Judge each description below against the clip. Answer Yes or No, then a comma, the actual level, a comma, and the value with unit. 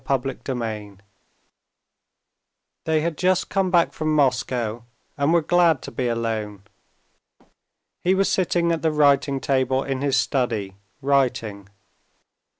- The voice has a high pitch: No, low, 135 Hz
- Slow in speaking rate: Yes, slow, 125 wpm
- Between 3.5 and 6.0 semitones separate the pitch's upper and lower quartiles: Yes, wide, 5.4 semitones